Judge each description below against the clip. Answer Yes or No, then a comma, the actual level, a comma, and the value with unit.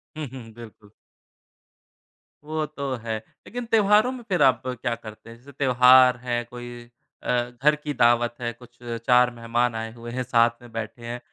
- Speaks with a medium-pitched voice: No, low, 120 Hz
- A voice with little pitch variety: Yes, narrow, 2.3 semitones